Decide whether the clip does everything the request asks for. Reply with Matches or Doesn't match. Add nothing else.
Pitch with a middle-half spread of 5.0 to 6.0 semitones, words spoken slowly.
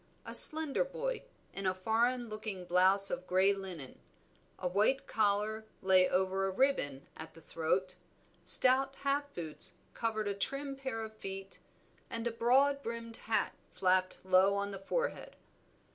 Doesn't match